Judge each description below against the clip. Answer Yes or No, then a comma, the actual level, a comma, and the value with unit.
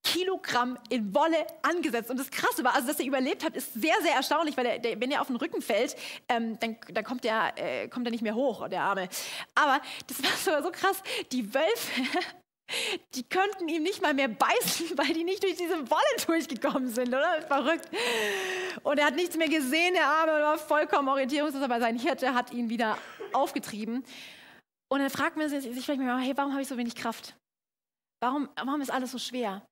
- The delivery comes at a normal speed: No, fast, 200 wpm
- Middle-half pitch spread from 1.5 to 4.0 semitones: No, average, 4.7 semitones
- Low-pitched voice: No, very high, 280 Hz